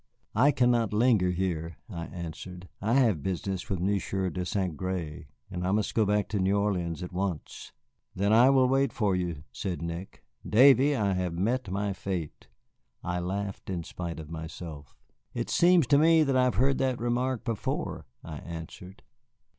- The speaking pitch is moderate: No, very low, 95 Hz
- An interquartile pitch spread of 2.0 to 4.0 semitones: No, average, 5.3 semitones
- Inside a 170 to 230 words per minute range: Yes, average, 175 wpm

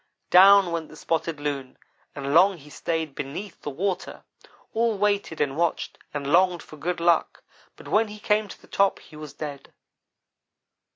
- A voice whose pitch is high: No, medium, 170 Hz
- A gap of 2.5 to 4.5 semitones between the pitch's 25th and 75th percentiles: No, average, 5.1 semitones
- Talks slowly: No, average, 170 wpm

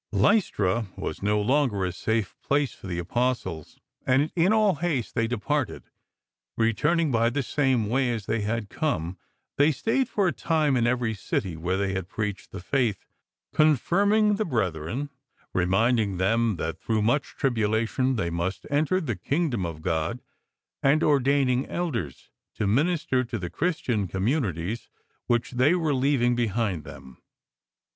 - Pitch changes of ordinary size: No, wide, 6.6 semitones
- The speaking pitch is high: No, low, 120 Hz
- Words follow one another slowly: No, average, 150 wpm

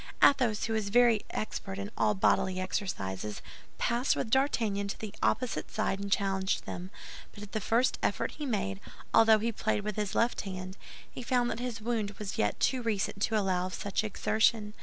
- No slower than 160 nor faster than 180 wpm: No, average, 190 wpm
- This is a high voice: Yes, high, 210 Hz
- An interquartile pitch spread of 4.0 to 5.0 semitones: No, average, 3.0 semitones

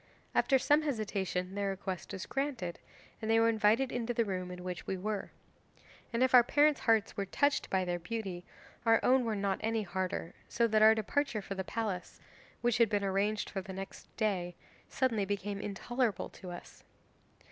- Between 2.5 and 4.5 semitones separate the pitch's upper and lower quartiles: Yes, average, 3.4 semitones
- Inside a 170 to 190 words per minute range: Yes, average, 185 wpm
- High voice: Yes, high, 210 Hz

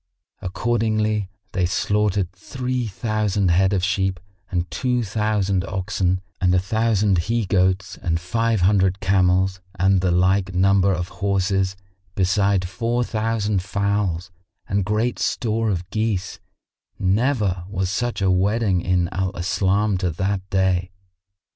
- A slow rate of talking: Yes, slow, 130 wpm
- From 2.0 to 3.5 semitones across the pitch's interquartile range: Yes, narrow, 2.6 semitones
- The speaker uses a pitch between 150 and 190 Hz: No, very low, 95 Hz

